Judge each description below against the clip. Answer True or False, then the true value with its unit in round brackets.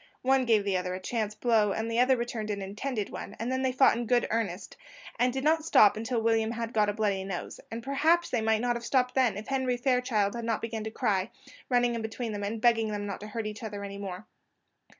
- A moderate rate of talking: False (250 wpm)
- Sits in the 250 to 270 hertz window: False (225 Hz)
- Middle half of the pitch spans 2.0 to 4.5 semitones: True (2.8 semitones)